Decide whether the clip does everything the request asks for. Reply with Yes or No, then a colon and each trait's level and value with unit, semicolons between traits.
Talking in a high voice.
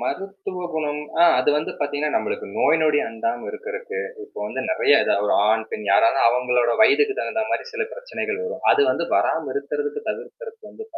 Yes: high, 200 Hz